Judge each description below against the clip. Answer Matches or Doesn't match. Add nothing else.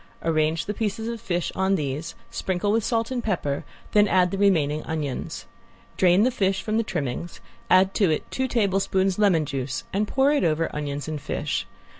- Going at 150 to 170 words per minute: Doesn't match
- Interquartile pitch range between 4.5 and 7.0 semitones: Matches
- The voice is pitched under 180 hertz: Doesn't match